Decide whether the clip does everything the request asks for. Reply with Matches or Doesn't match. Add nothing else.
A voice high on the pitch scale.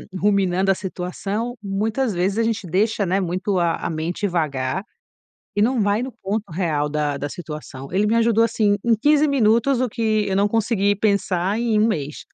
Matches